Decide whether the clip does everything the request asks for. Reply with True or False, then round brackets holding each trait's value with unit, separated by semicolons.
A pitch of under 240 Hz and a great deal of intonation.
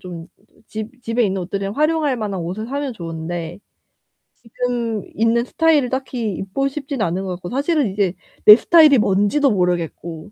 True (220 Hz; 6.2 semitones)